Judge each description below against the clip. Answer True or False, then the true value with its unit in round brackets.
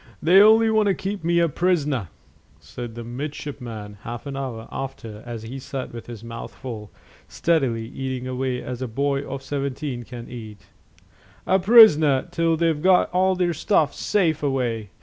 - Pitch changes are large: True (5.9 semitones)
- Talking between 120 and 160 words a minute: False (170 wpm)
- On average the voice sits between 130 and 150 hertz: True (135 Hz)